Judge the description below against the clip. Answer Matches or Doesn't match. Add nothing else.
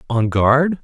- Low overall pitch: Matches